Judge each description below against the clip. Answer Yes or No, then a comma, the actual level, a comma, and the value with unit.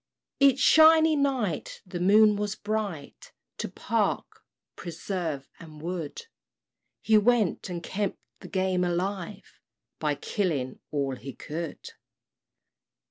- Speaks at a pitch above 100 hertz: Yes, medium, 185 Hz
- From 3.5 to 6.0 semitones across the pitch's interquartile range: Yes, average, 4.6 semitones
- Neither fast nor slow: No, slow, 110 wpm